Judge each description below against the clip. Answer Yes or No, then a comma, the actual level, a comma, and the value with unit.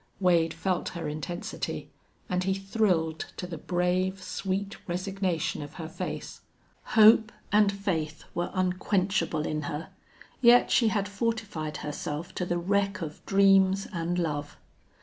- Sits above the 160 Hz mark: Yes, medium, 185 Hz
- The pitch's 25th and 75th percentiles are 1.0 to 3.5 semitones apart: Yes, average, 3.2 semitones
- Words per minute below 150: Yes, slow, 135 wpm